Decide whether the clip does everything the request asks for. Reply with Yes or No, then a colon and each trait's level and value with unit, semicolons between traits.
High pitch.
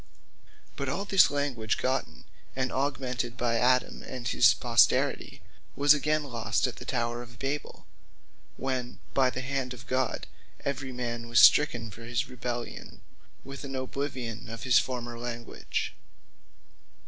No: low, 125 Hz